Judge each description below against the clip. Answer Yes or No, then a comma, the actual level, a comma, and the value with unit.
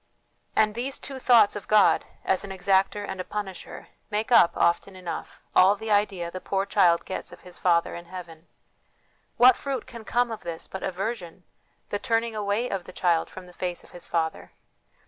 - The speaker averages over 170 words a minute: Yes, average, 190 wpm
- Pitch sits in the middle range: No, high, 195 Hz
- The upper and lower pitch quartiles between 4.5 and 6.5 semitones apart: No, average, 3.7 semitones